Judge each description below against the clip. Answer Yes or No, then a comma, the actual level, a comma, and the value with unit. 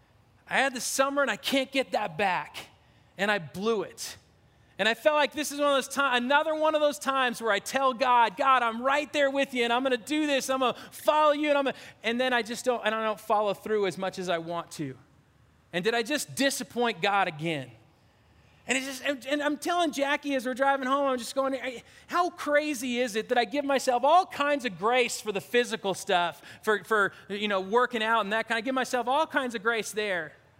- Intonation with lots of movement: No, average, 4.5 semitones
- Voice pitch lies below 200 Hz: No, high, 245 Hz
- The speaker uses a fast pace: Yes, fast, 240 wpm